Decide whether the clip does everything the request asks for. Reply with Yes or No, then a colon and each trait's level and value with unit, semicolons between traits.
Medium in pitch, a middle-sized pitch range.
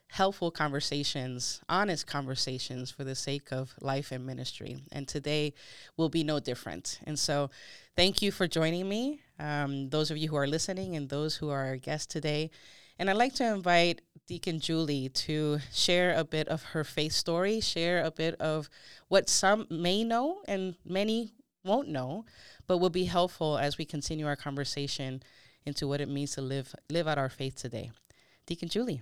Yes: medium, 155 Hz; average, 3.9 semitones